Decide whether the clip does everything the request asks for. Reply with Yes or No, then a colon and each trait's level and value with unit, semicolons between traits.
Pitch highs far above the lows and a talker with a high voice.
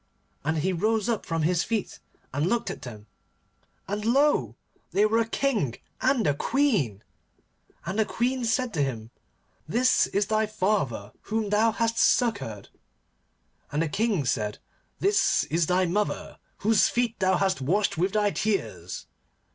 Yes: wide, 6.3 semitones; high, 205 Hz